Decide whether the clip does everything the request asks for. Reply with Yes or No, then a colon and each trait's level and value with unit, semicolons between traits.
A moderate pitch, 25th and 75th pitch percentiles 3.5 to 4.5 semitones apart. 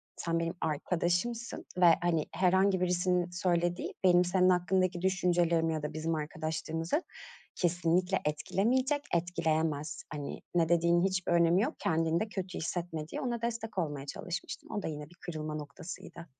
No: medium, 175 Hz; narrow, 2.4 semitones